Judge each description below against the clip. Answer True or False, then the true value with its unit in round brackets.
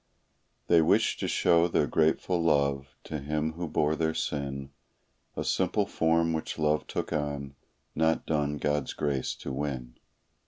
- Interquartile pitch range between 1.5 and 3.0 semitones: True (2.4 semitones)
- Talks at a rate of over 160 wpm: False (150 wpm)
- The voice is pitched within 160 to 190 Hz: False (75 Hz)